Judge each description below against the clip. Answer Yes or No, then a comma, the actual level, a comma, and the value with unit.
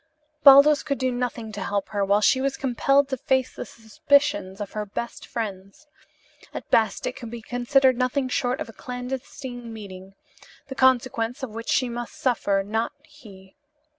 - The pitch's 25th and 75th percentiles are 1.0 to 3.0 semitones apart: No, average, 3.6 semitones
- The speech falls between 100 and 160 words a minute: No, average, 170 wpm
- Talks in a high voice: Yes, high, 245 Hz